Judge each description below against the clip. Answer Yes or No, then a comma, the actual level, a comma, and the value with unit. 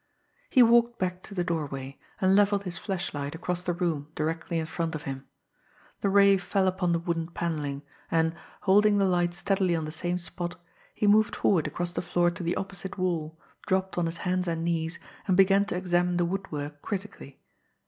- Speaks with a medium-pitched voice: Yes, medium, 175 Hz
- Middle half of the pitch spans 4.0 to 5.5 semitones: No, average, 2.7 semitones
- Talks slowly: No, average, 190 wpm